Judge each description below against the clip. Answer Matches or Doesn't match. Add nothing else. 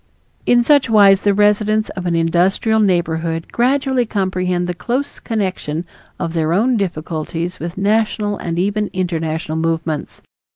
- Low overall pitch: Doesn't match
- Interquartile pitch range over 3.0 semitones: Matches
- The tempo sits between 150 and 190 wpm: Doesn't match